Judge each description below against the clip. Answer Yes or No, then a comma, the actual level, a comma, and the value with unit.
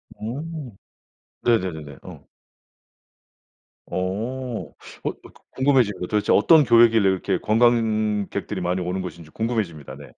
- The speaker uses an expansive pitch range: No, average, 4.5 semitones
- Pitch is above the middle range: No, low, 105 Hz